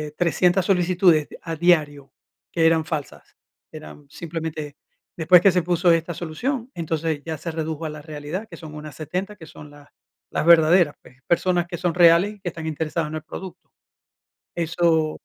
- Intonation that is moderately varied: No, narrow, 2.2 semitones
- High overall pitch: No, medium, 165 Hz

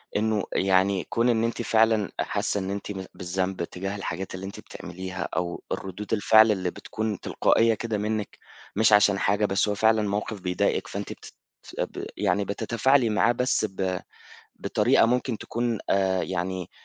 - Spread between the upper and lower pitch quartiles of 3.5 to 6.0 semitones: No, average, 2.8 semitones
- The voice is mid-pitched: No, low, 100 Hz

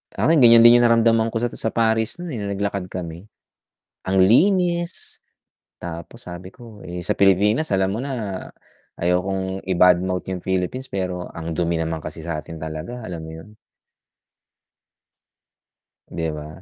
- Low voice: Yes, very low, 95 Hz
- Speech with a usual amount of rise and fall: Yes, average, 4.9 semitones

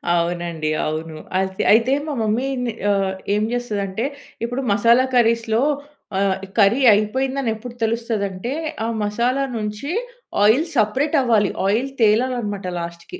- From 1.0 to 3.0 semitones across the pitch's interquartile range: No, average, 3.6 semitones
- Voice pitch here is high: Yes, high, 220 Hz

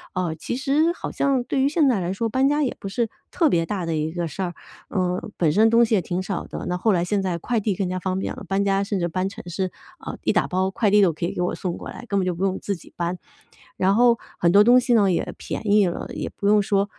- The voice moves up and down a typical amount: Yes, average, 3.9 semitones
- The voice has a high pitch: Yes, high, 195 Hz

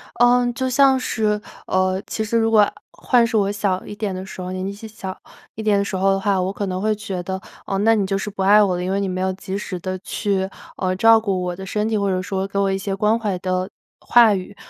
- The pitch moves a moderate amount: No, narrow, 2.3 semitones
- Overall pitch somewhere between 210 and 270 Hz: No, high, 200 Hz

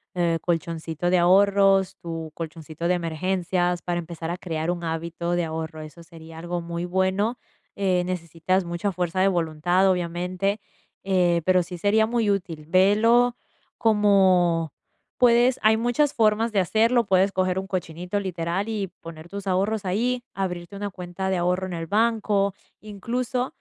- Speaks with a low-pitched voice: No, medium, 185 Hz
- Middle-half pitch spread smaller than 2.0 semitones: No, average, 2.9 semitones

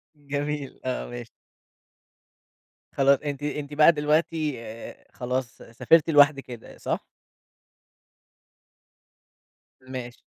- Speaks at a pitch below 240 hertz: Yes, medium, 140 Hz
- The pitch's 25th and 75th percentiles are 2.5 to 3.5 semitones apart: Yes, average, 2.8 semitones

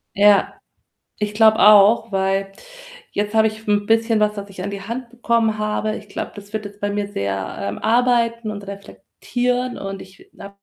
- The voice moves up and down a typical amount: No, narrow, 2.0 semitones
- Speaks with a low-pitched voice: No, high, 210 Hz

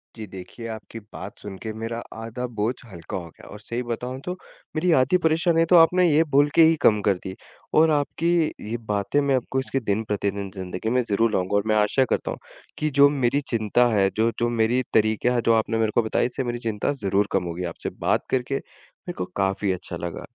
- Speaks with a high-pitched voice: No, low, 115 Hz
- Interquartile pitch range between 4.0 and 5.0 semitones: Yes, average, 4.6 semitones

